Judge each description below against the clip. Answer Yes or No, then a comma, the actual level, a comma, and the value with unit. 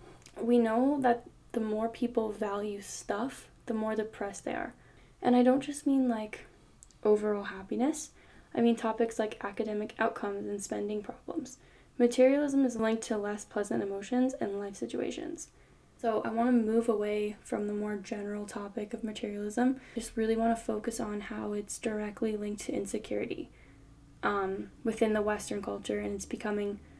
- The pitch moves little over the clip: Yes, narrow, 2.2 semitones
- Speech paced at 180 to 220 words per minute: No, average, 160 wpm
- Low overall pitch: No, high, 220 Hz